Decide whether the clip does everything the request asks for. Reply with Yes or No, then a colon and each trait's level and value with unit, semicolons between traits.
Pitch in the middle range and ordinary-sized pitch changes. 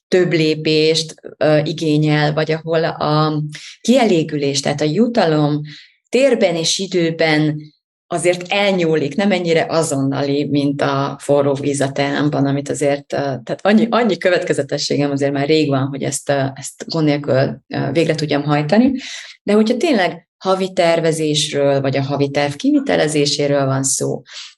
Yes: medium, 155 Hz; average, 3.3 semitones